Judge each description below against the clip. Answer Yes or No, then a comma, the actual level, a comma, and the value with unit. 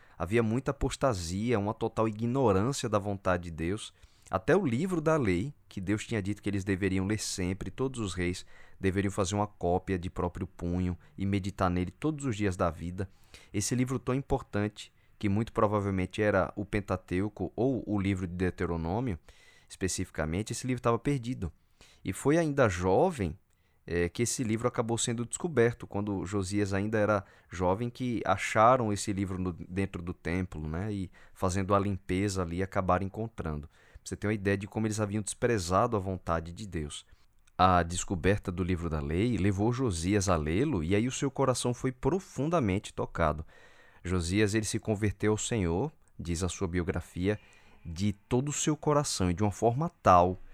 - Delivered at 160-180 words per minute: Yes, average, 175 wpm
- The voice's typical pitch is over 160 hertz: No, low, 100 Hz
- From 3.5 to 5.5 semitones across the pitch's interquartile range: Yes, average, 3.8 semitones